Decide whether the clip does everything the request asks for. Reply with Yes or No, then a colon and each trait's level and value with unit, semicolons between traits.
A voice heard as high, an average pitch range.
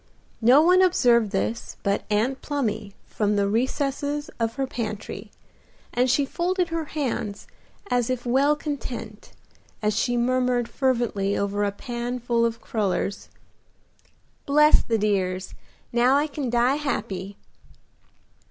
Yes: high, 240 Hz; average, 4.6 semitones